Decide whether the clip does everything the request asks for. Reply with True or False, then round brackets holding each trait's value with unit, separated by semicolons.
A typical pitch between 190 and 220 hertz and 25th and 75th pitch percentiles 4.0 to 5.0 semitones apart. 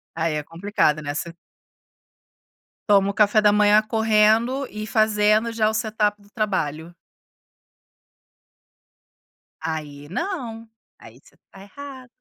True (210 Hz; 4.4 semitones)